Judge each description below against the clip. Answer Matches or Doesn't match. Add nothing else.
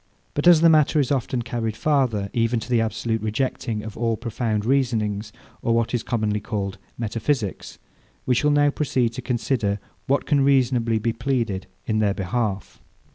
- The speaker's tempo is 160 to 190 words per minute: Matches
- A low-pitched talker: Matches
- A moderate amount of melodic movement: Matches